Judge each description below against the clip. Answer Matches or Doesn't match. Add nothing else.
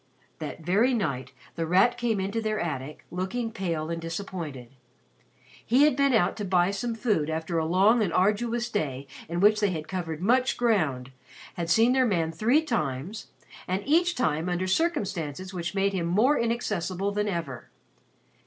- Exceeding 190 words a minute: Doesn't match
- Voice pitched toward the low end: Doesn't match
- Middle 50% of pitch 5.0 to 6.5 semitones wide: Matches